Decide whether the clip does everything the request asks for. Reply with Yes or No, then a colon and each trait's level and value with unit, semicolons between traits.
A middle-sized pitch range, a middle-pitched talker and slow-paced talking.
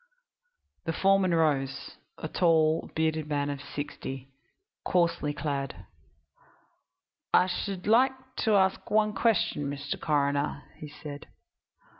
Yes: average, 4.6 semitones; medium, 155 Hz; slow, 110 wpm